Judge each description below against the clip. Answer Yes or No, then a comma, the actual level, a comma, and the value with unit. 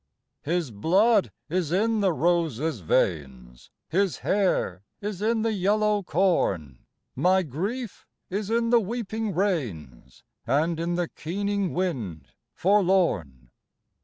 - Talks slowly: Yes, slow, 115 wpm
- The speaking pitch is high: No, medium, 180 Hz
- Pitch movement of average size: No, wide, 7.4 semitones